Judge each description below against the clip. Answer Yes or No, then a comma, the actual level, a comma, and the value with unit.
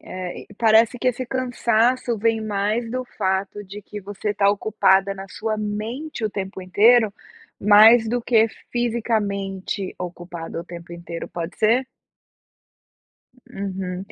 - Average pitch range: Yes, average, 3.2 semitones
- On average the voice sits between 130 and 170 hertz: No, high, 210 Hz